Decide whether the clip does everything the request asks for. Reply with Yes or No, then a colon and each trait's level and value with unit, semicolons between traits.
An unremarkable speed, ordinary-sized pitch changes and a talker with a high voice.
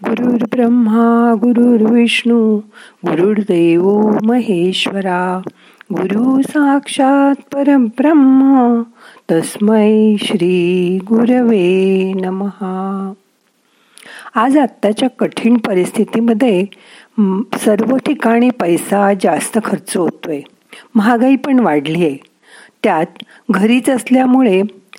No: slow, 65 wpm; average, 4.2 semitones; high, 225 Hz